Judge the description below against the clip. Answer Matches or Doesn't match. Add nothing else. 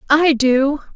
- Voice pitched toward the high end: Matches